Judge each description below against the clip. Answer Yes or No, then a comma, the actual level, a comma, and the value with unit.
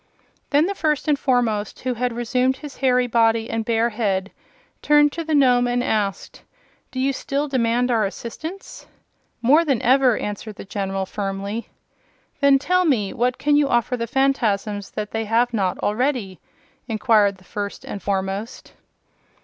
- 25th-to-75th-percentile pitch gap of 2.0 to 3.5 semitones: No, average, 4.4 semitones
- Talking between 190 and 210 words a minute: No, average, 160 wpm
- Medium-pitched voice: No, high, 240 Hz